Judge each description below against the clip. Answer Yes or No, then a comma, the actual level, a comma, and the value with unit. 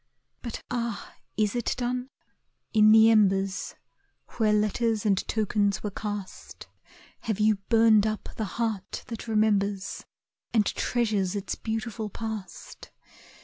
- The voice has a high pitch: Yes, high, 215 Hz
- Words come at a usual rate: No, slow, 120 wpm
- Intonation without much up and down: Yes, narrow, 1.7 semitones